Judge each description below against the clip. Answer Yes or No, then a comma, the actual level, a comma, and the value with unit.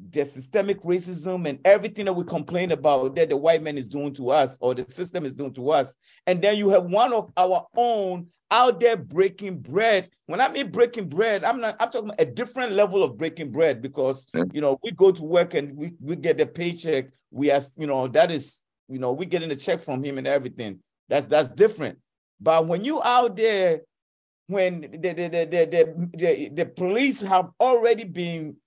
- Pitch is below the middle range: No, medium, 175 Hz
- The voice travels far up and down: Yes, wide, 5.9 semitones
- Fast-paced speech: Yes, fast, 210 wpm